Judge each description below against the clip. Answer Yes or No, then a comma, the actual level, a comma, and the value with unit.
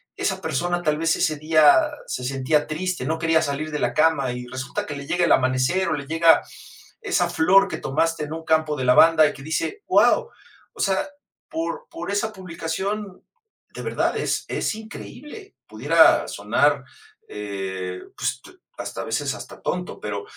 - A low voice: No, medium, 160 Hz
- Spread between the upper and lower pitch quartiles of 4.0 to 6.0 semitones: Yes, average, 5.3 semitones